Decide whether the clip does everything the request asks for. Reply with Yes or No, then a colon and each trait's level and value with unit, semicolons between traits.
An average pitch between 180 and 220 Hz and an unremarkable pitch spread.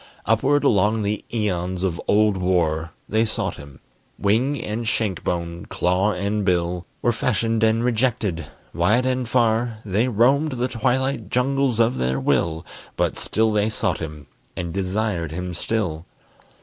No: low, 105 Hz; average, 4.8 semitones